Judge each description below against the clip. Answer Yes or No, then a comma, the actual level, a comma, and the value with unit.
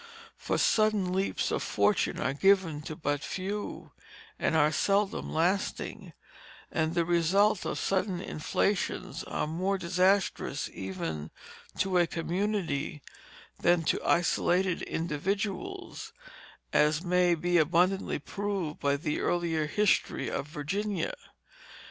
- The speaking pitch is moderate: Yes, medium, 175 Hz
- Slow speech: Yes, slow, 115 wpm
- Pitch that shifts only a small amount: No, average, 3.9 semitones